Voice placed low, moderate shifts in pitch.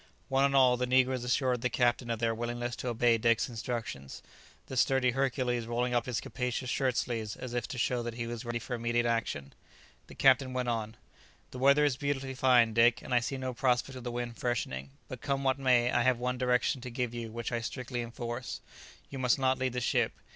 No: low, 125 Hz; narrow, 1.6 semitones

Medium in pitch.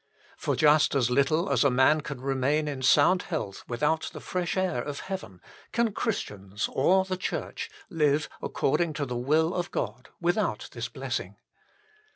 Yes: medium, 150 Hz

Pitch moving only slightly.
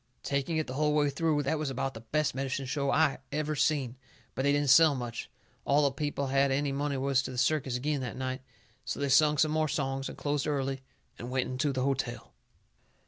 Yes: narrow, 2.0 semitones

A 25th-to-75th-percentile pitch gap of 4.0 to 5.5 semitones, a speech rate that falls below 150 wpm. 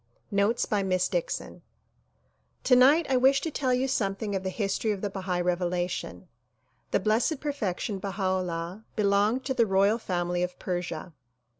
No: average, 5.2 semitones; average, 155 wpm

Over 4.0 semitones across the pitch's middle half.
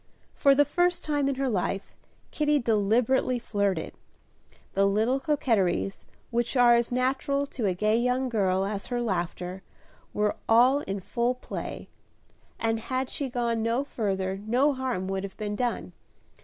Yes: average, 4.6 semitones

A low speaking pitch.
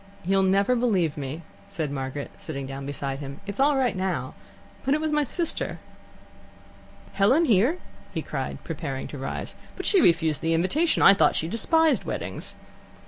No: high, 190 Hz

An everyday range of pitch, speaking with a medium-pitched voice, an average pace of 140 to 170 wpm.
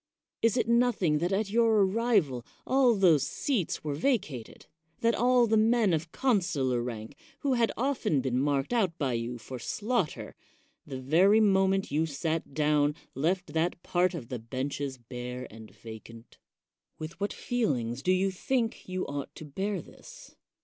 No: wide, 8.4 semitones; medium, 170 Hz; average, 165 wpm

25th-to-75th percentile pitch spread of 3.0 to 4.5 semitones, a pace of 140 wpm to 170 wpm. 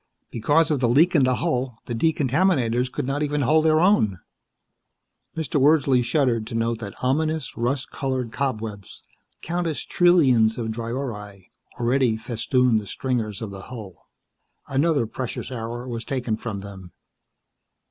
Yes: average, 4.2 semitones; average, 145 wpm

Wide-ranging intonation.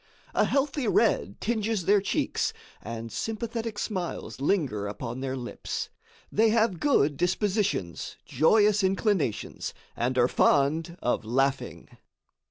Yes: wide, 8.9 semitones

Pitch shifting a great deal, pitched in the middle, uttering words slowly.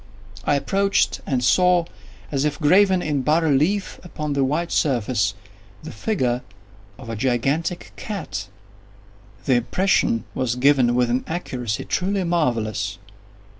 Yes: wide, 6.0 semitones; medium, 145 Hz; slow, 130 wpm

